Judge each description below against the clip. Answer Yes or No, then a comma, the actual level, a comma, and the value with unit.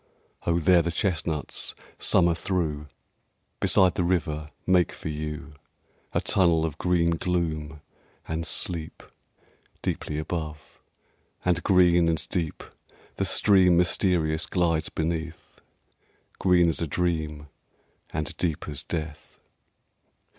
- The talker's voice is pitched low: Yes, very low, 85 Hz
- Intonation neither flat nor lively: No, narrow, 2.2 semitones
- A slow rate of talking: Yes, slow, 110 wpm